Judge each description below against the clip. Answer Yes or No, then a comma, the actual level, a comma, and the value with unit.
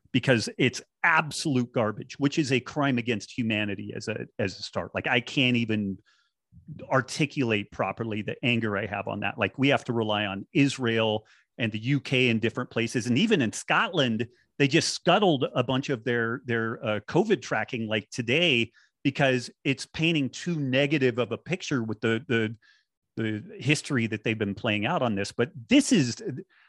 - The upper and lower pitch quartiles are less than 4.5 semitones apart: Yes, average, 4.1 semitones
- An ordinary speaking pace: Yes, average, 180 wpm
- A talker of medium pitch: No, low, 120 Hz